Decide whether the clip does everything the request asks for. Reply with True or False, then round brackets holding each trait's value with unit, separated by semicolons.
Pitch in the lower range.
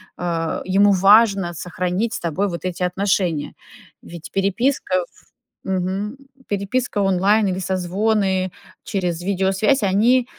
False (190 Hz)